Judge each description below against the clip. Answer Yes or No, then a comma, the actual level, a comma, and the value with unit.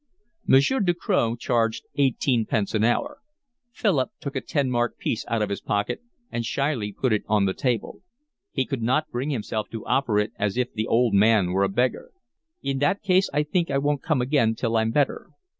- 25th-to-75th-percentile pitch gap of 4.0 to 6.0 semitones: Yes, average, 4.4 semitones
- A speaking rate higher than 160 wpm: Yes, average, 200 wpm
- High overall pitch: No, low, 120 Hz